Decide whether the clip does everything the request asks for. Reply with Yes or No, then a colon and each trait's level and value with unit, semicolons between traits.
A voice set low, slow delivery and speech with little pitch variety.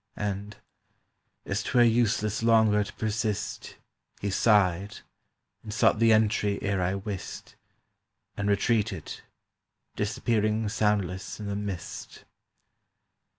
Yes: low, 105 Hz; slow, 105 wpm; narrow, 1.7 semitones